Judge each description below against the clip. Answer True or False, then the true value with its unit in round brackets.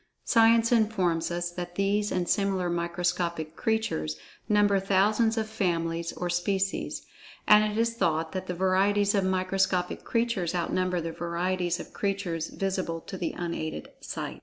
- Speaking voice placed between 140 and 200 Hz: True (185 Hz)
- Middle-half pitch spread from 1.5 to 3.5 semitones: True (3.0 semitones)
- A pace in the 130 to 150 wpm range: True (140 wpm)